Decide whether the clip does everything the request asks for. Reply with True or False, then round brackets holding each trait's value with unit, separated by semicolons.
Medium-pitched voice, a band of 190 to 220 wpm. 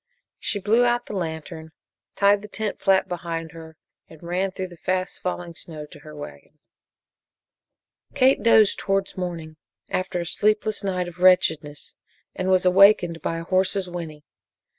False (180 Hz; 155 wpm)